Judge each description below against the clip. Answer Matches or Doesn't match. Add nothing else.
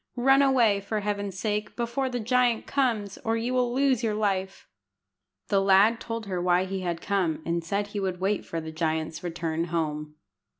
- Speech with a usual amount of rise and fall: Matches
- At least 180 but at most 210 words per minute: Matches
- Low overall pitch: Doesn't match